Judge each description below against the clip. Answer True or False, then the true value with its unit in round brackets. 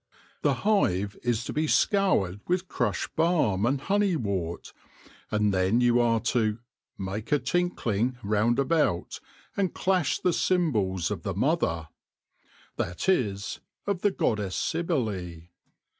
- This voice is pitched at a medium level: False (120 Hz)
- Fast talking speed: False (145 wpm)